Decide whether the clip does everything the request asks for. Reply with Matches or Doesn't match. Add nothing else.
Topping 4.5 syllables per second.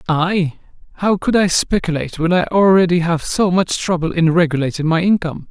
Matches